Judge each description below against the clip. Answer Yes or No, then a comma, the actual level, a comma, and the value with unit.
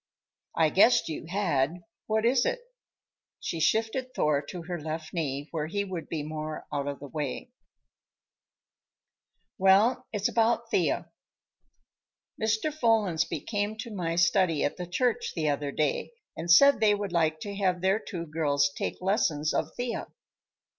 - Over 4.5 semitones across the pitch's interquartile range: Yes, wide, 5.6 semitones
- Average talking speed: Yes, average, 155 wpm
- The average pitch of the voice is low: No, medium, 175 Hz